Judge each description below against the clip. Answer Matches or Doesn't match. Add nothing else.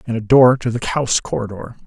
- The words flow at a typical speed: Doesn't match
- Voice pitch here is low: Matches